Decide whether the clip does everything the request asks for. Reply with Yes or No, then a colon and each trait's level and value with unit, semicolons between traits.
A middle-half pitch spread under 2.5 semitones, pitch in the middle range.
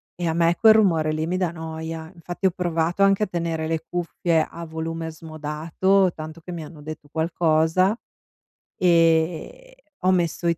Yes: narrow, 1.8 semitones; medium, 165 Hz